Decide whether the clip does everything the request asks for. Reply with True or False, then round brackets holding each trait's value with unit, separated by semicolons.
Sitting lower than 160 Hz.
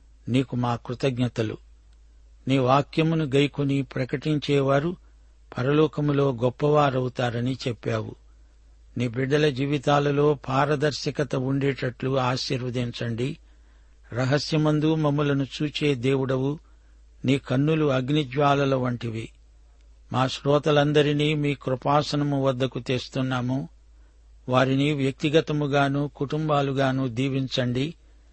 True (135 Hz)